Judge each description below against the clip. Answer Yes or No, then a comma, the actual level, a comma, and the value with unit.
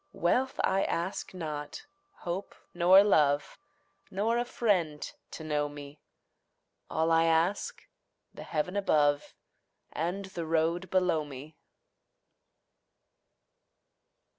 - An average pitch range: Yes, average, 3.9 semitones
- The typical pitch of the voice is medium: Yes, medium, 165 Hz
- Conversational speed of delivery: No, slow, 100 wpm